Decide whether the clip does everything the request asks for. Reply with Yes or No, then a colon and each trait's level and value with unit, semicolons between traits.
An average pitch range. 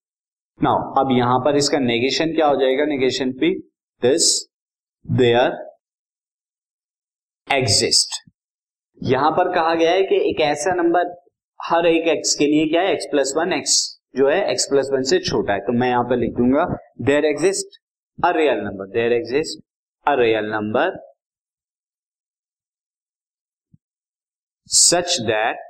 No: wide, 5.9 semitones